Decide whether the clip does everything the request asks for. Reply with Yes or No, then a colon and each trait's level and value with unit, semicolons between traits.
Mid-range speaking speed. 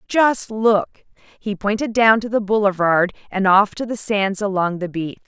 Yes: average, 180 wpm